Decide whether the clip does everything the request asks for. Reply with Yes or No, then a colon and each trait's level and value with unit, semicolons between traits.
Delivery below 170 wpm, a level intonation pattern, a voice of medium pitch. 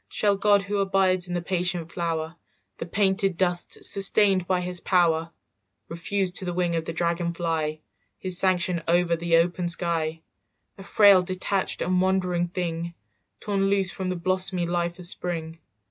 Yes: average, 160 wpm; narrow, 1.8 semitones; medium, 180 Hz